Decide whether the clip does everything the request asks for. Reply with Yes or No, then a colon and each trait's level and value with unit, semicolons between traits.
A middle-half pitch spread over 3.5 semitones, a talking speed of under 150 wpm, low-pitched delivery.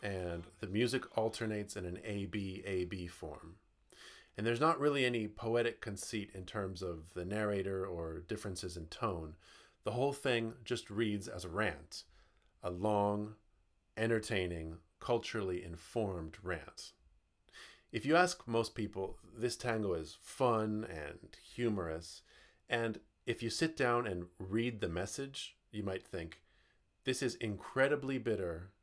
Yes: average, 4.2 semitones; average, 140 wpm; low, 105 Hz